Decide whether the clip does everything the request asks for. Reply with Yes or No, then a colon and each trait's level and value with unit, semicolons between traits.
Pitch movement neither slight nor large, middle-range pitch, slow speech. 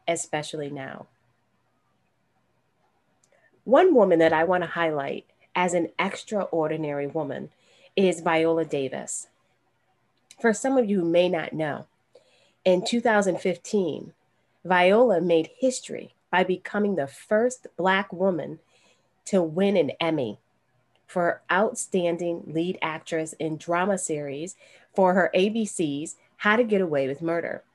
Yes: average, 3.4 semitones; medium, 175 Hz; slow, 120 wpm